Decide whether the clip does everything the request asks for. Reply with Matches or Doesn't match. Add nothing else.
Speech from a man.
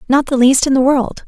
Doesn't match